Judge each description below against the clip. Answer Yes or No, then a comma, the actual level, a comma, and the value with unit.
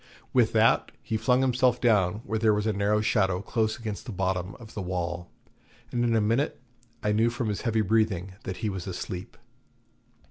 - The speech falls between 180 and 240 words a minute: Yes, average, 190 wpm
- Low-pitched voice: Yes, low, 105 Hz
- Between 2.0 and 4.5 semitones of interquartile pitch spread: Yes, average, 3.2 semitones